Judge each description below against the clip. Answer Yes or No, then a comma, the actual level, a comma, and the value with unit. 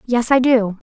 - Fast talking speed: No, average, 195 wpm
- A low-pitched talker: No, high, 235 Hz